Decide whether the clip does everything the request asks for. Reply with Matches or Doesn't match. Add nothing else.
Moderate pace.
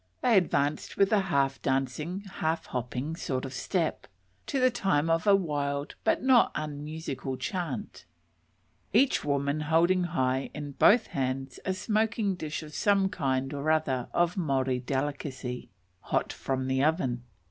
Matches